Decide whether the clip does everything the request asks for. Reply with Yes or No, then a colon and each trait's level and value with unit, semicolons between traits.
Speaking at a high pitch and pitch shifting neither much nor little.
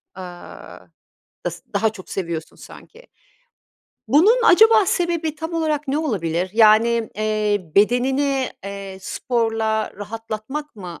No: high, 225 Hz; wide, 6.9 semitones